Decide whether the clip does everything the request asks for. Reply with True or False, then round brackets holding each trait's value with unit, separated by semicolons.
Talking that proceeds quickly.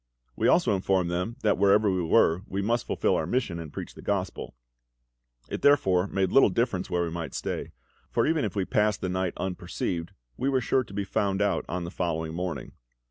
True (210 wpm)